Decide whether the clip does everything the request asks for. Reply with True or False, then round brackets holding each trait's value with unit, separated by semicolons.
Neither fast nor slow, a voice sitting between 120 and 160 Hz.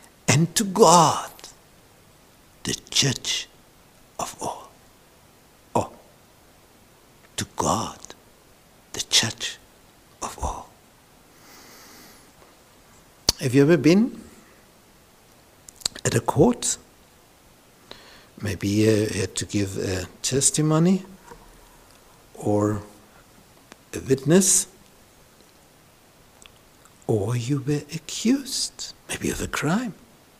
False (75 wpm; 140 Hz)